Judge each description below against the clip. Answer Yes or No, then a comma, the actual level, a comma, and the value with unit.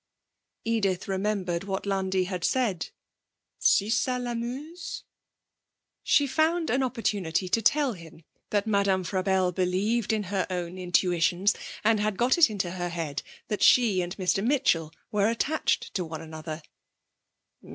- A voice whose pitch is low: No, high, 195 Hz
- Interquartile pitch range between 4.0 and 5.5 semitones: Yes, average, 4.3 semitones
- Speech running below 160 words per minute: Yes, average, 140 wpm